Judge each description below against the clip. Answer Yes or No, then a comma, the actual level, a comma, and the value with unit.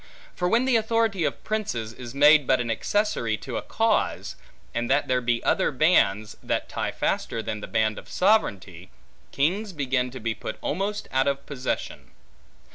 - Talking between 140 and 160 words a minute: No, average, 175 wpm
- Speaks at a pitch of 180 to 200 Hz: No, low, 135 Hz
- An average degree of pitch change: No, wide, 8.3 semitones